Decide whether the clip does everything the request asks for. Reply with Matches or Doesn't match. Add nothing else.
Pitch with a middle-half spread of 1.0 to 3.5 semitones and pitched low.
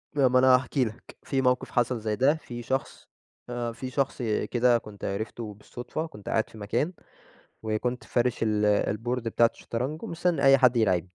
Matches